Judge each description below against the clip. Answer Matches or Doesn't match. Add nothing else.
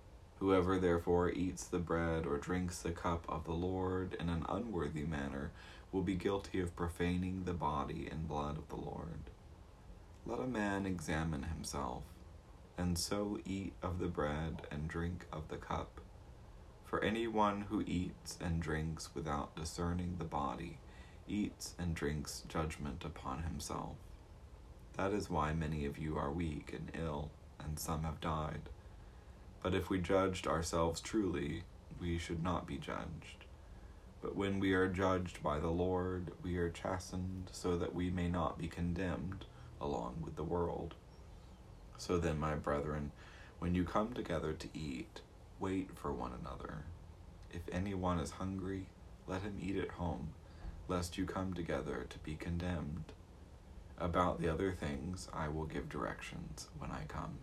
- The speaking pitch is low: Matches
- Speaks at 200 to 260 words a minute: Doesn't match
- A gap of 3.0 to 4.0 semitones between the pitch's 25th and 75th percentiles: Doesn't match